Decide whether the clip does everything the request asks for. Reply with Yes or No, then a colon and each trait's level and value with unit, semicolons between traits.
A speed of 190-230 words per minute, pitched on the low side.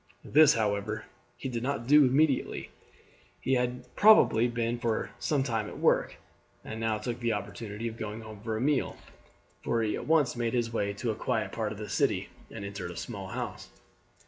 Yes: average, 195 wpm; low, 115 Hz